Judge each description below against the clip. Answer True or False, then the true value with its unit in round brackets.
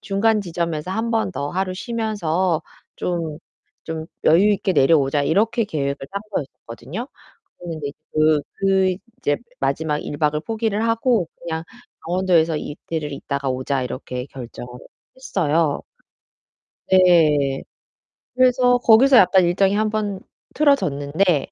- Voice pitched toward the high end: False (170 Hz)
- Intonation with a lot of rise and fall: True (5.7 semitones)